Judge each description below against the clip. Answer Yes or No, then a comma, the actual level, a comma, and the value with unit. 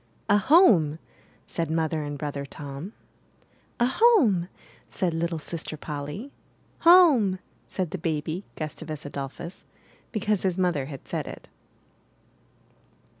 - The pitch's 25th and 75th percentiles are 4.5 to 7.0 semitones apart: Yes, average, 5.2 semitones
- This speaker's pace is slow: Yes, slow, 120 wpm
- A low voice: No, medium, 170 Hz